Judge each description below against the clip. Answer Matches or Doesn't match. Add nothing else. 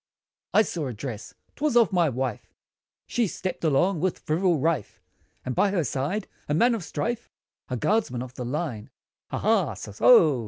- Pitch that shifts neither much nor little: Doesn't match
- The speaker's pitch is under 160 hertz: Doesn't match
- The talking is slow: Doesn't match